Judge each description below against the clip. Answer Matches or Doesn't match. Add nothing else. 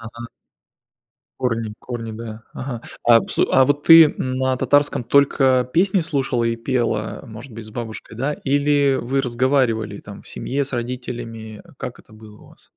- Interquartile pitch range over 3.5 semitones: Doesn't match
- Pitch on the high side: Doesn't match